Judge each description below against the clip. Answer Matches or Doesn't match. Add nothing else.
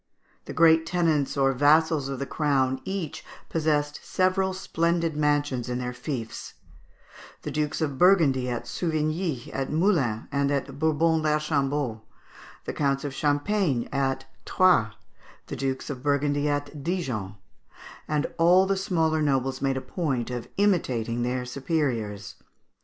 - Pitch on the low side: Doesn't match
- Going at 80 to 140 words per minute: Matches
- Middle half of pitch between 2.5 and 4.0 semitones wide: Matches